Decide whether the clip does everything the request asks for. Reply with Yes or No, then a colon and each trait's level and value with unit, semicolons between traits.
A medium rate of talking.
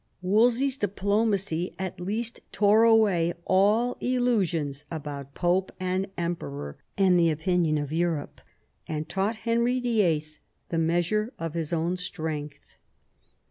No: slow, 120 wpm